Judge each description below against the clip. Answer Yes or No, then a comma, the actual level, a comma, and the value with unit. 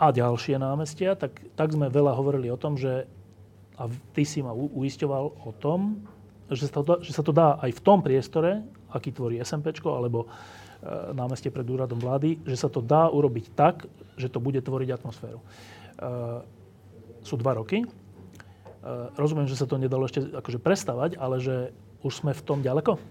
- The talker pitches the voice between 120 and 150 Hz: Yes, low, 130 Hz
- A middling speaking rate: No, fast, 180 wpm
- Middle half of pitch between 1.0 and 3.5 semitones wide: No, average, 4.0 semitones